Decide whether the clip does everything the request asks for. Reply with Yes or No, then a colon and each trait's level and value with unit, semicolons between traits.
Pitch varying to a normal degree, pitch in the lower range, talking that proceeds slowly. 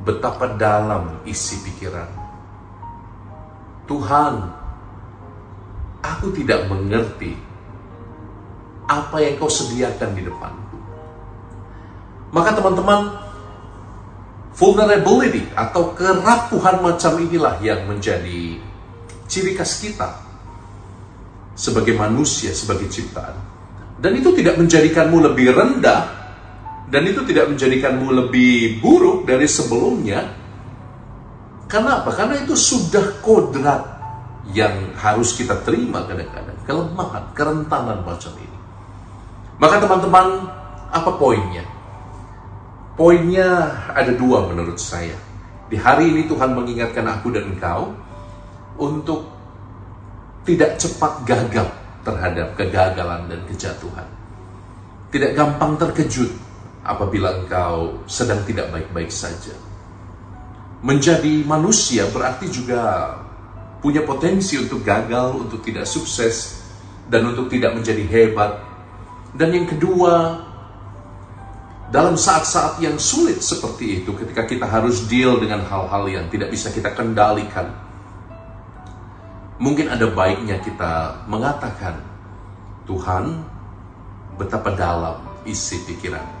No: average, 4.6 semitones; low, 105 Hz; average, 95 wpm